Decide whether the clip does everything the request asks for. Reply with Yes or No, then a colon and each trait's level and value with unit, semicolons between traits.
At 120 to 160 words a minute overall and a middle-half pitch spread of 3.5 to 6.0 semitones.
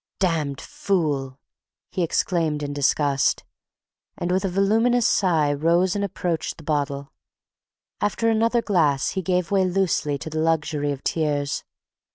Yes: average, 140 wpm; average, 4.7 semitones